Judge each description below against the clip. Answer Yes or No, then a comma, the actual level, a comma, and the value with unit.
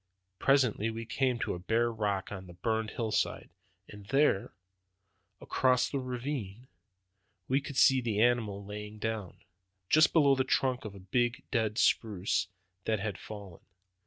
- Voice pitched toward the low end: Yes, low, 110 Hz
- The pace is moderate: Yes, average, 155 wpm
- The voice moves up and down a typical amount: Yes, average, 3.8 semitones